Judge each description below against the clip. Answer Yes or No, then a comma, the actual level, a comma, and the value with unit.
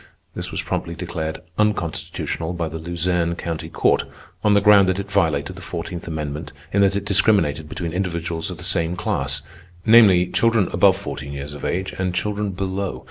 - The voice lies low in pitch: Yes, very low, 90 Hz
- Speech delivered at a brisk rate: No, average, 175 wpm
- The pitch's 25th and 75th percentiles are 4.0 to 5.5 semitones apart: No, average, 3.3 semitones